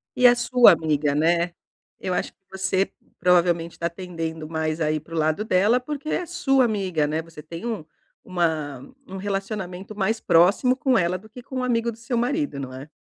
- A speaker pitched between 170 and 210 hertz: Yes, medium, 185 Hz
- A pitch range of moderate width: No, wide, 6.2 semitones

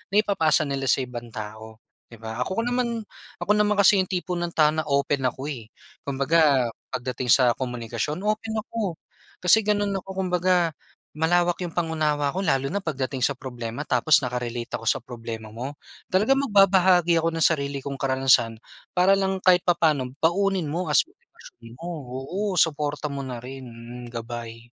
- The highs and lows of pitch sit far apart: Yes, wide, 6.7 semitones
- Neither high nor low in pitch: Yes, medium, 150 Hz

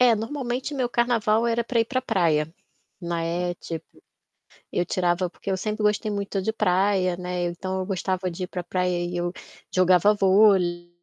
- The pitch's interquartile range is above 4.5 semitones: No, average, 3.6 semitones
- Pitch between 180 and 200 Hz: Yes, medium, 185 Hz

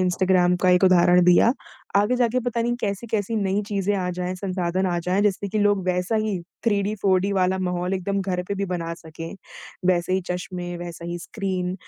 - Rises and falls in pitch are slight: Yes, narrow, 2.1 semitones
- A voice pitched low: No, medium, 185 Hz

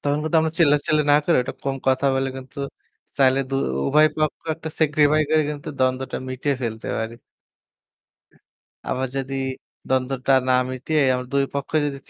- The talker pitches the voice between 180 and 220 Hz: No, medium, 140 Hz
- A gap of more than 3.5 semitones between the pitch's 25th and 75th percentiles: No, narrow, 2.6 semitones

